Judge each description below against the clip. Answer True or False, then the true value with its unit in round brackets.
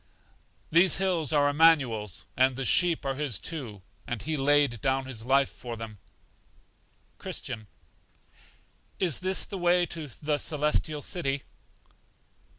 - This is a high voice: False (145 Hz)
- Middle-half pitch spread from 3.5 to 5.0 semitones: True (4.5 semitones)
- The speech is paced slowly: True (130 wpm)